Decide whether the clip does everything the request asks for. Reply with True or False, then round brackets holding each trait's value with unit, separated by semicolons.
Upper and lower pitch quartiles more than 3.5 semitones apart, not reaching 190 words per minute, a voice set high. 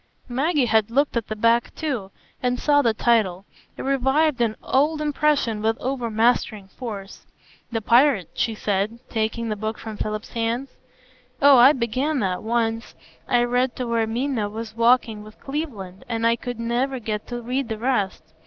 False (3.2 semitones; 170 wpm; 235 Hz)